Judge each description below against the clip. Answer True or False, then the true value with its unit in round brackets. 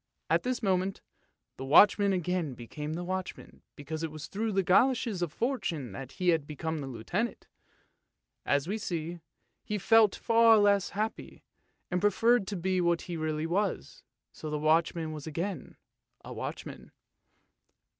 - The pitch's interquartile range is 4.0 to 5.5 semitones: True (4.7 semitones)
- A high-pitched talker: False (175 Hz)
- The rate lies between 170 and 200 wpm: False (160 wpm)